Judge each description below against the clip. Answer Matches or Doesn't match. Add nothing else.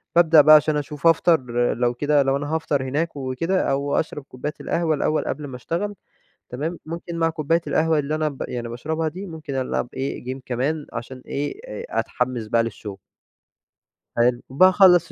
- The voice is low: Doesn't match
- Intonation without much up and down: Doesn't match